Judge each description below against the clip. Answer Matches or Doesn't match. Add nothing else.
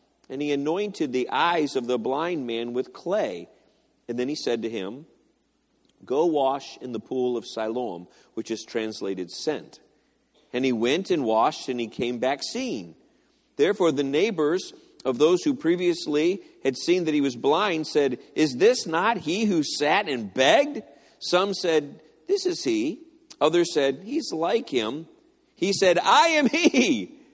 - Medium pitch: Matches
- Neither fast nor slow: Matches